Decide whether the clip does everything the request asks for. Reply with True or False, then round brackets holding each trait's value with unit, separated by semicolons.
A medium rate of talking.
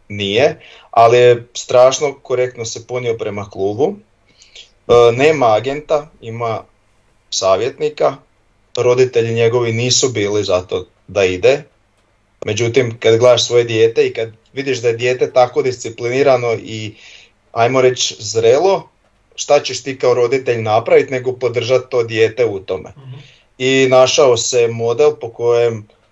True (125 wpm)